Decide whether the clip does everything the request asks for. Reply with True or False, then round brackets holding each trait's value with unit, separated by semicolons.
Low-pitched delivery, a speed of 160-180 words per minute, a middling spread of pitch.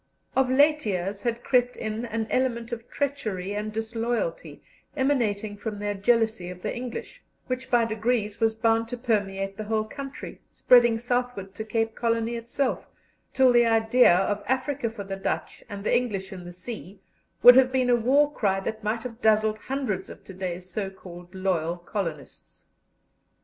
False (225 Hz; 170 wpm; 3.6 semitones)